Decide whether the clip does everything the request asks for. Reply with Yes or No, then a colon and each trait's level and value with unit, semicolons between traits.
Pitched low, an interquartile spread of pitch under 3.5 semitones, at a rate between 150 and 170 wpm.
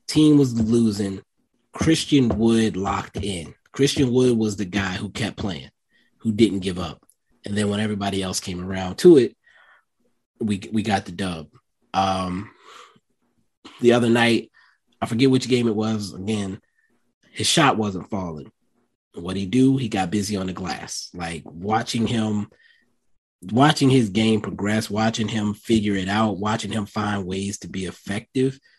Yes: low, 105 Hz; average, 2.9 semitones; average, 160 wpm